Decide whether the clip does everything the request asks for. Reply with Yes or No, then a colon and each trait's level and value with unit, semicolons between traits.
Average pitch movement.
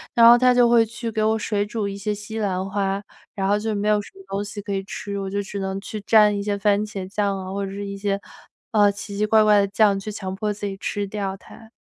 No: narrow, 1.3 semitones